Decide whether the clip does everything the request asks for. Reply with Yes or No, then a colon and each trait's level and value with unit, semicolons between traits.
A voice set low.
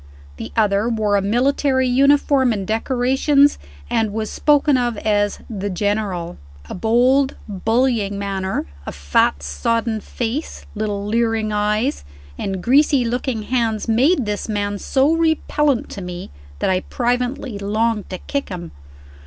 No: high, 225 Hz